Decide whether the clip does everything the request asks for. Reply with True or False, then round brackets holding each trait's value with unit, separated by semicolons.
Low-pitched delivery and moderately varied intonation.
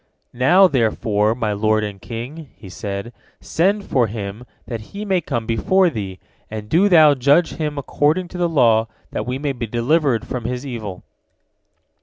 False (125 Hz; 6.2 semitones)